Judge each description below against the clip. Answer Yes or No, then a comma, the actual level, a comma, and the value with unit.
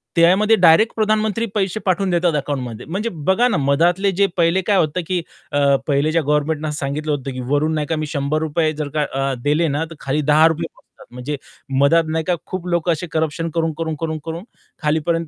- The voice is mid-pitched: Yes, medium, 160 Hz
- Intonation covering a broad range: No, average, 3.0 semitones